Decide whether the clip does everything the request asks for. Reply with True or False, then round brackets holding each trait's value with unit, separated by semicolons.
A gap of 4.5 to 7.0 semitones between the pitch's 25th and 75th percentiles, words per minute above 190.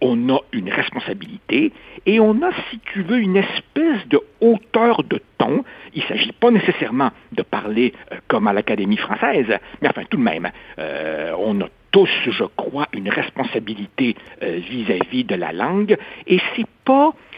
False (5.3 semitones; 165 wpm)